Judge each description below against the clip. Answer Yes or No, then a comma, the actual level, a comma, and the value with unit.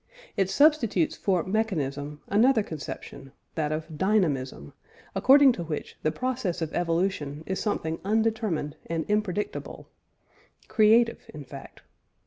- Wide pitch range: Yes, wide, 6.0 semitones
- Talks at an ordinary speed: No, slow, 115 wpm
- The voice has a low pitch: No, medium, 180 Hz